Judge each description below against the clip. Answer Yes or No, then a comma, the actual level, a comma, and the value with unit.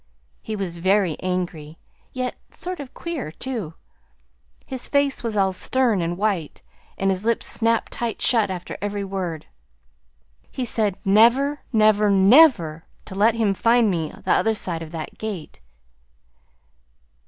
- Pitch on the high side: Yes, high, 205 Hz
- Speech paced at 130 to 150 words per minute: Yes, average, 140 wpm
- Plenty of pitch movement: No, average, 4.3 semitones